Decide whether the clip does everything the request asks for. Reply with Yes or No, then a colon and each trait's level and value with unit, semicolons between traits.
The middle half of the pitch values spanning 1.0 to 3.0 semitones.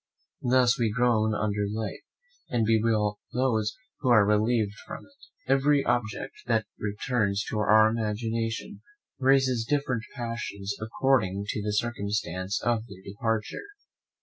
Yes: narrow, 2.6 semitones